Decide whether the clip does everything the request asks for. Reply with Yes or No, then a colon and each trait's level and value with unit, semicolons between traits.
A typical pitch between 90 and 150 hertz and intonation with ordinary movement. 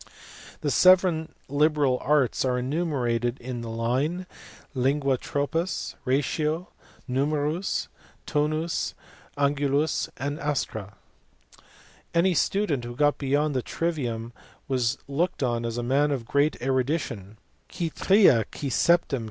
Yes: medium, 140 Hz; average, 3.7 semitones